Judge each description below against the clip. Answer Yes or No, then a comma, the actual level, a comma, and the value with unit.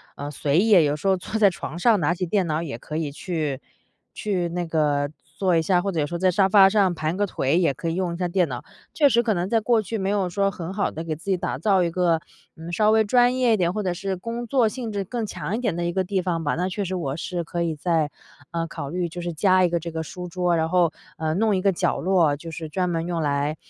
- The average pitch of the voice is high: No, medium, 180 Hz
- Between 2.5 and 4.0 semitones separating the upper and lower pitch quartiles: Yes, average, 3.3 semitones